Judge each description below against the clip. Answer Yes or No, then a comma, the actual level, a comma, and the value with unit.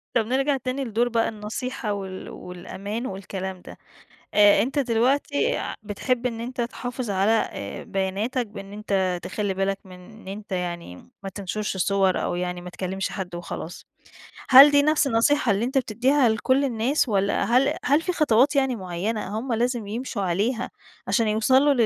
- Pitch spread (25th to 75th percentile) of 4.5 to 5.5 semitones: Yes, average, 4.9 semitones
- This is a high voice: Yes, high, 220 Hz